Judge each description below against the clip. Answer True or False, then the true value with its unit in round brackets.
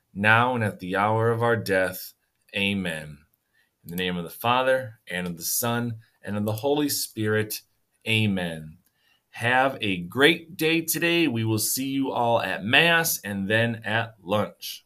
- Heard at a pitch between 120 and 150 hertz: False (110 Hz)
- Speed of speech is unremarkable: True (165 wpm)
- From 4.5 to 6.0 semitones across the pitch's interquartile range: True (4.8 semitones)